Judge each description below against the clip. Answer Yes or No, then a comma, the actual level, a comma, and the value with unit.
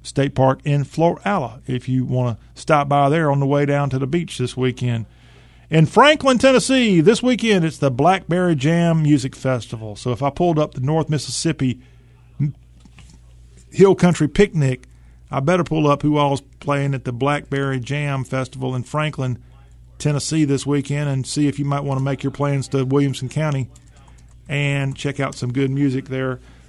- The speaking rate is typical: Yes, average, 180 wpm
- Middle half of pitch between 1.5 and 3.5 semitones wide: Yes, average, 3.0 semitones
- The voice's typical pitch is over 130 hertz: Yes, medium, 140 Hz